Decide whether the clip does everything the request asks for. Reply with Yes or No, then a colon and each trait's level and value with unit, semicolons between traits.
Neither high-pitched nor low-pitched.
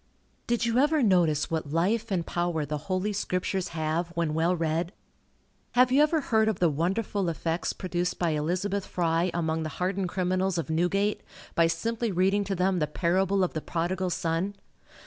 Yes: medium, 180 Hz